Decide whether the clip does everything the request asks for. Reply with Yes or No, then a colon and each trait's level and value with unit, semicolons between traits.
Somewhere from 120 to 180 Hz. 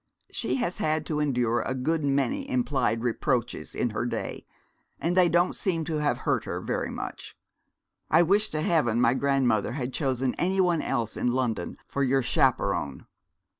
Yes: medium, 140 Hz